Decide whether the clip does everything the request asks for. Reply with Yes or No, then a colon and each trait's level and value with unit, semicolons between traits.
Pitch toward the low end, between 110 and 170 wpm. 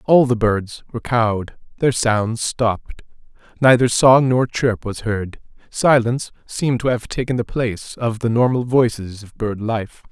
Yes: low, 115 Hz; average, 160 wpm